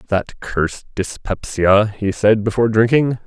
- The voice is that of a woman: No, male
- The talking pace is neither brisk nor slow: No, slow, 130 wpm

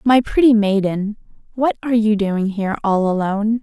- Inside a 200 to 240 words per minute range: No, average, 165 wpm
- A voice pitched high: Yes, high, 215 Hz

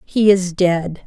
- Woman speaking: Yes, female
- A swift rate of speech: No, average, 170 wpm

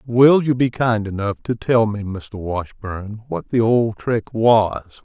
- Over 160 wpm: Yes, average, 180 wpm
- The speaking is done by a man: Yes, male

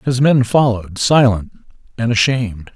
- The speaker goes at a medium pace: No, slow, 130 wpm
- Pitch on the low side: Yes, low, 115 Hz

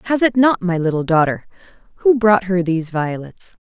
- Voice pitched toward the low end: No, high, 190 Hz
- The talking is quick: No, average, 180 wpm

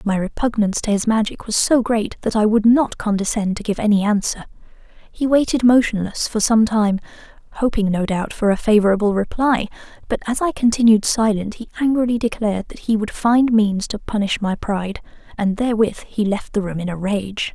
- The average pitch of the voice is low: No, high, 215 Hz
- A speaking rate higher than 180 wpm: Yes, average, 190 wpm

